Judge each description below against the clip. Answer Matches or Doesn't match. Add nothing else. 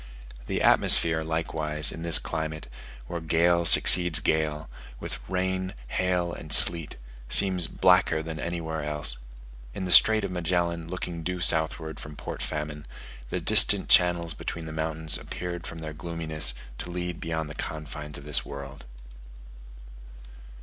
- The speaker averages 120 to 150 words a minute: Matches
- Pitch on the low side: Matches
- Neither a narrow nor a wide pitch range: Doesn't match